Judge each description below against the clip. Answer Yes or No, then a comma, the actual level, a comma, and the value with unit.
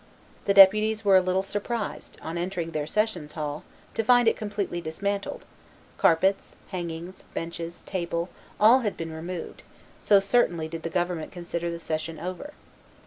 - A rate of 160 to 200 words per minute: No, average, 150 wpm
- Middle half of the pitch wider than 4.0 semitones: No, average, 3.5 semitones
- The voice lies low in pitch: No, medium, 180 Hz